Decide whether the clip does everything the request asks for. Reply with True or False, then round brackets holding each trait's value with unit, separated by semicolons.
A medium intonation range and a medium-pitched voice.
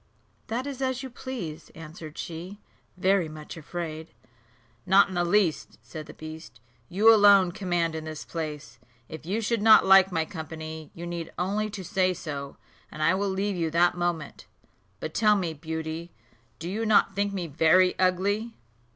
True (4.0 semitones; 175 Hz)